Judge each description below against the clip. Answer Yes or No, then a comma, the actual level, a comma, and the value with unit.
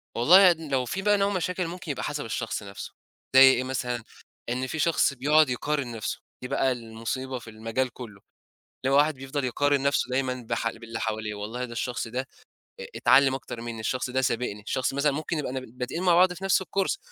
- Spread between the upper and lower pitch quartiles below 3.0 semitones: No, average, 4.0 semitones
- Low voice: Yes, low, 130 Hz